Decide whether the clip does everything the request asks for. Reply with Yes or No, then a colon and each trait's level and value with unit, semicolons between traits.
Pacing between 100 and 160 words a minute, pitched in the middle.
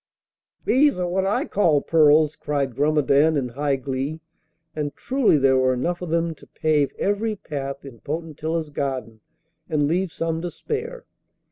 Yes: average, 155 wpm; medium, 155 Hz